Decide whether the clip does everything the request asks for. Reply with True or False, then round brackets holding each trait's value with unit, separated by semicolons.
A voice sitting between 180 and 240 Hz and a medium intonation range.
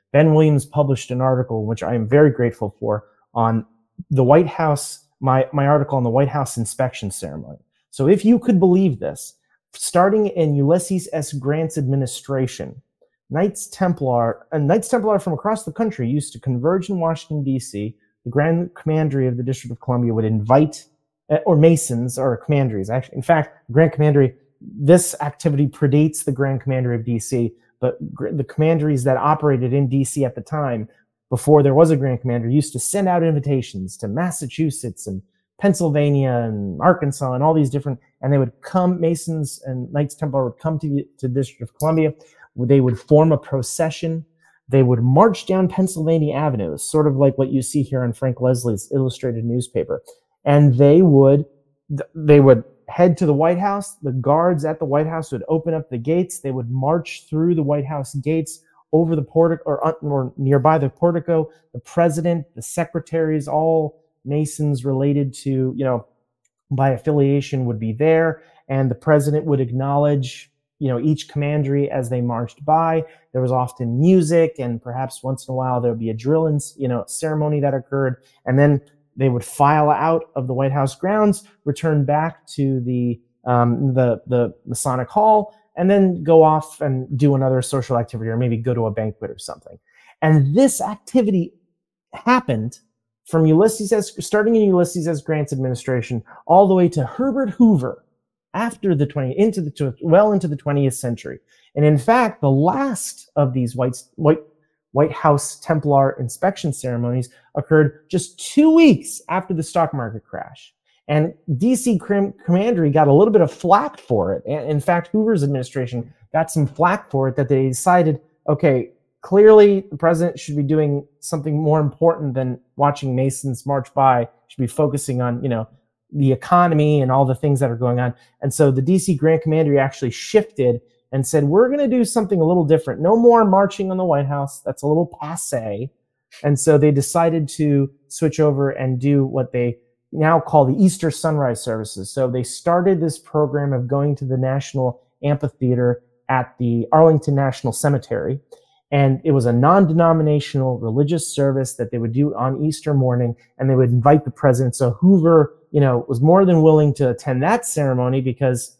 False (145 Hz; 3.9 semitones)